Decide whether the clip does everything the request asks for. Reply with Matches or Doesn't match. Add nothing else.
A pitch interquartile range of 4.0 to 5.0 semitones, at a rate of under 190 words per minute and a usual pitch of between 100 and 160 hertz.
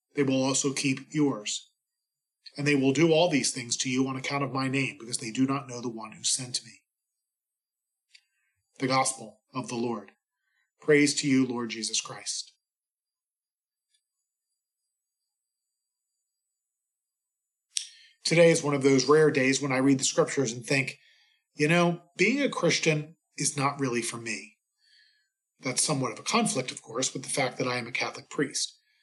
Doesn't match